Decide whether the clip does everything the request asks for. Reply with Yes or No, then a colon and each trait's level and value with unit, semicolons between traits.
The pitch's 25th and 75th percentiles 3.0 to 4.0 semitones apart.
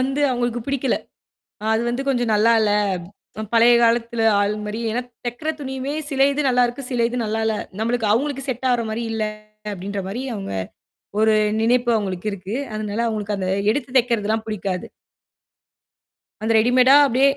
No: narrow, 2.6 semitones